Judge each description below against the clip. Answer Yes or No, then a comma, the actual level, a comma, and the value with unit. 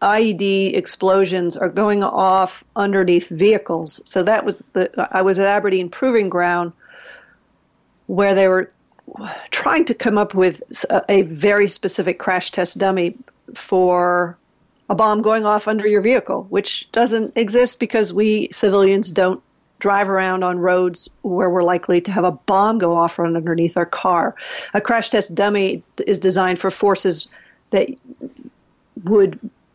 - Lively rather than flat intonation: No, narrow, 2.6 semitones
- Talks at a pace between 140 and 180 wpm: Yes, average, 150 wpm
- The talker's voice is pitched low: No, high, 195 Hz